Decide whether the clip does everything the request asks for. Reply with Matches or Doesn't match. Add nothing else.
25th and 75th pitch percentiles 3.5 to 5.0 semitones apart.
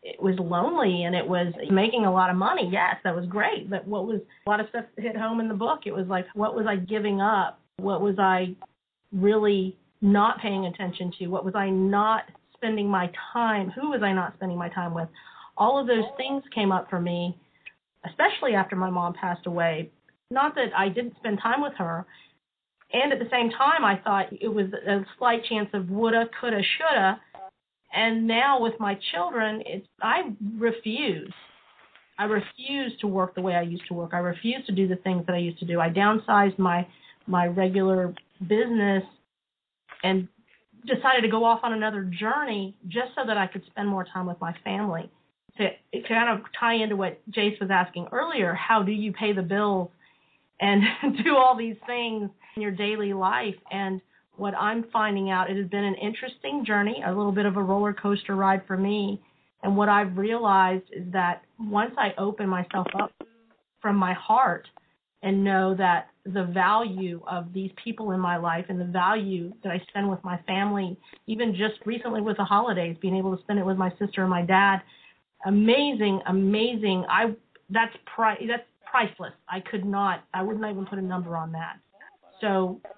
Doesn't match